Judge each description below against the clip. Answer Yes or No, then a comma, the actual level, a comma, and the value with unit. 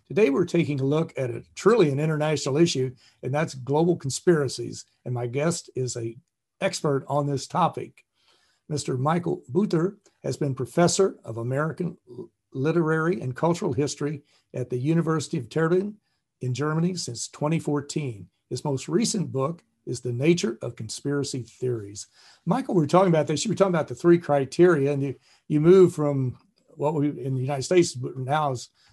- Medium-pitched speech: Yes, medium, 145 Hz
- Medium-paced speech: Yes, average, 170 wpm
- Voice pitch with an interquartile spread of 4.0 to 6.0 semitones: Yes, average, 4.6 semitones